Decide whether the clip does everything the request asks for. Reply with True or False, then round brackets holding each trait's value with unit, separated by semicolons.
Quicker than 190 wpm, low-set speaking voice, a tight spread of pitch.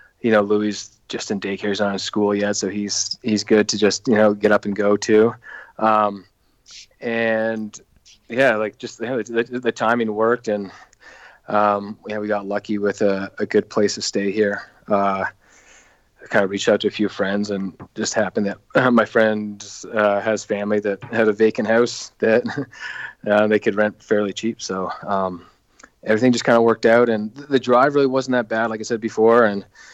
True (200 wpm; 105 Hz; 1.8 semitones)